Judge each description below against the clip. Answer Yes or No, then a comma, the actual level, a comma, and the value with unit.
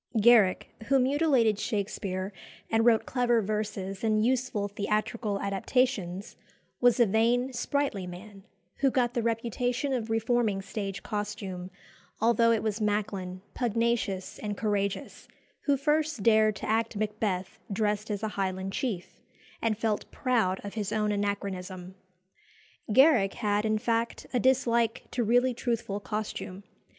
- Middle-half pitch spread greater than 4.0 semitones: No, average, 3.0 semitones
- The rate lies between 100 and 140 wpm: Yes, slow, 135 wpm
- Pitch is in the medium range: No, high, 215 Hz